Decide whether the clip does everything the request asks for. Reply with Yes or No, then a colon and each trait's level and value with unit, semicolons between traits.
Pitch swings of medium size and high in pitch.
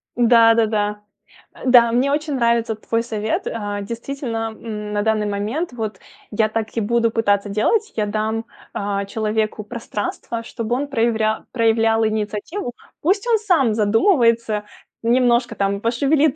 No: narrow, 2.2 semitones; high, 225 Hz